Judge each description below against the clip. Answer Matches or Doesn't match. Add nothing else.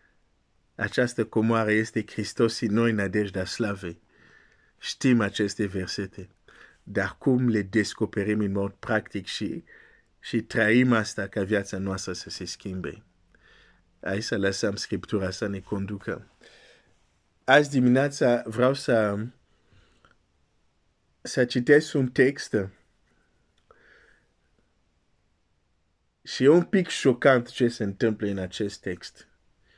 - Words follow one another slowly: Matches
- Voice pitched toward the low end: Matches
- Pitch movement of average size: Matches